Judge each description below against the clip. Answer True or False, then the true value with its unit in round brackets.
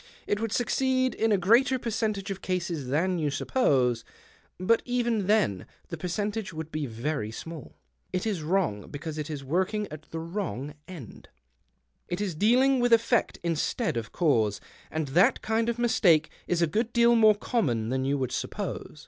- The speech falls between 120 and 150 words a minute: False (175 wpm)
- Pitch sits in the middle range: True (180 Hz)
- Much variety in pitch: True (6.8 semitones)